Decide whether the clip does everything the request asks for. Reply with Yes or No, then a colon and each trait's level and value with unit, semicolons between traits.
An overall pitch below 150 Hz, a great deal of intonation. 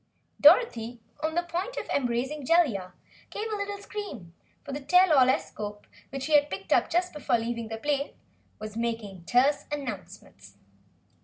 No: very high, 265 Hz; wide, 6.2 semitones